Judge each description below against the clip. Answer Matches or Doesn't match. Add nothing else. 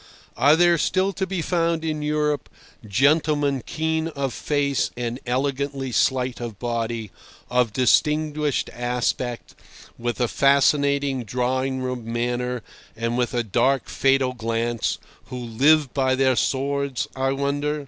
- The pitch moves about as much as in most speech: Matches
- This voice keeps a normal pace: Doesn't match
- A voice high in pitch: Doesn't match